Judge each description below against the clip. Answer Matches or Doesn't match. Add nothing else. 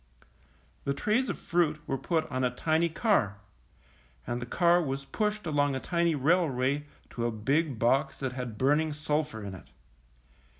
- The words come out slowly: Doesn't match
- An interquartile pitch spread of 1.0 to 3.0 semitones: Doesn't match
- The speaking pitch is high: Doesn't match